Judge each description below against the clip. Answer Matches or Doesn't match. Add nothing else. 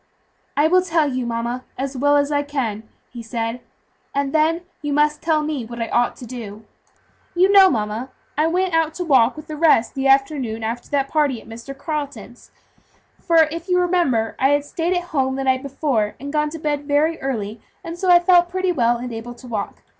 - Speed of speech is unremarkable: Doesn't match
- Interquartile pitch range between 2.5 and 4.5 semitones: Doesn't match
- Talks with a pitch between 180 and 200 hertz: Doesn't match